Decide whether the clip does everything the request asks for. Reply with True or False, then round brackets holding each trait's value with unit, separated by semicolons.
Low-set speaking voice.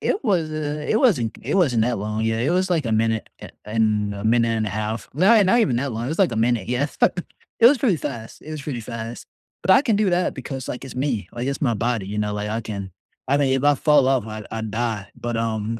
True (120 Hz)